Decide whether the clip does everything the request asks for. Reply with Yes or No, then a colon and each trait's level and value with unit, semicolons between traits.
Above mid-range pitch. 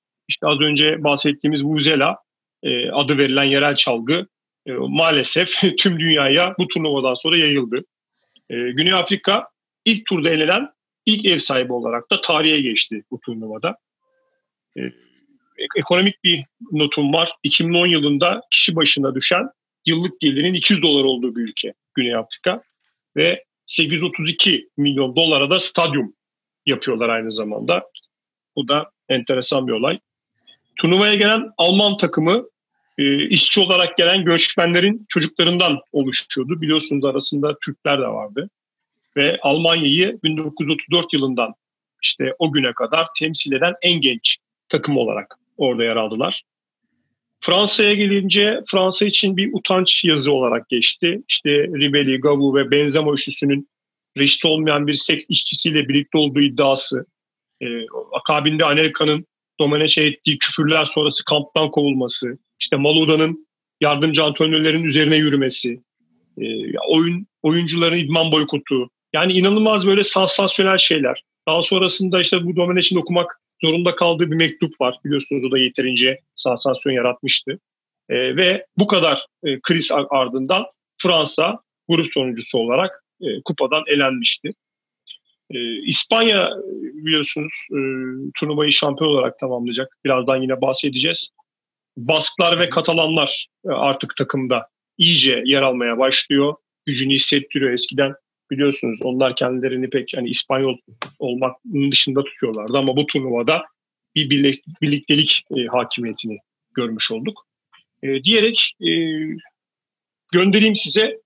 No: medium, 155 Hz